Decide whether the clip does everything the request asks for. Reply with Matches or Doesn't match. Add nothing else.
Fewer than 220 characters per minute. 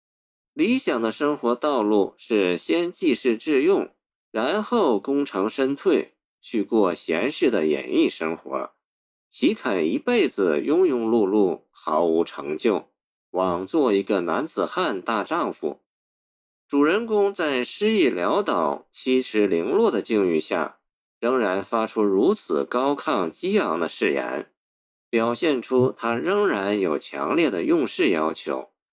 Matches